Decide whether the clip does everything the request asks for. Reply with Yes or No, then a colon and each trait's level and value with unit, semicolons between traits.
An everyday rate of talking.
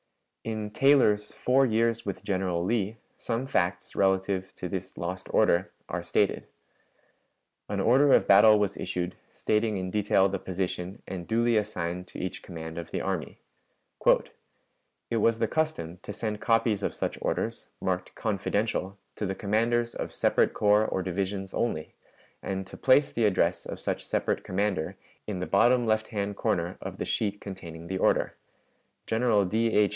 Yes: average, 160 wpm